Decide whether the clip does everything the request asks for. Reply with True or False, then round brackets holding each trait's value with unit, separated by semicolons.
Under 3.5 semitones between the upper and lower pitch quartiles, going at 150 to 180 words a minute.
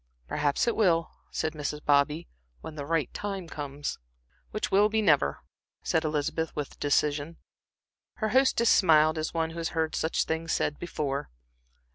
True (2.6 semitones; 155 wpm)